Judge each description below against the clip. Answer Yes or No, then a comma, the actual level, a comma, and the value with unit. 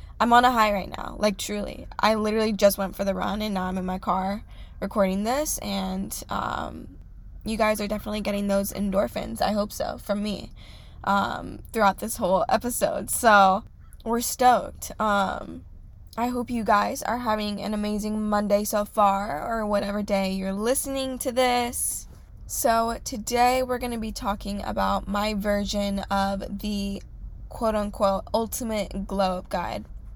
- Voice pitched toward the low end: No, high, 205 Hz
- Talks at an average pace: Yes, average, 160 wpm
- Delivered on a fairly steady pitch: Yes, narrow, 2.1 semitones